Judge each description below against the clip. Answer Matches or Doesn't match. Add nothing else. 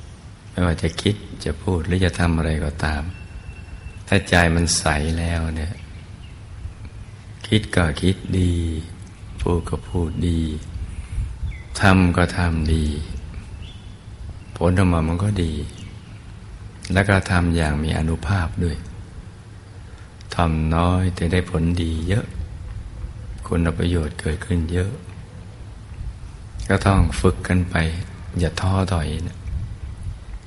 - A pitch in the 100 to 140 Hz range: Doesn't match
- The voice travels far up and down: Doesn't match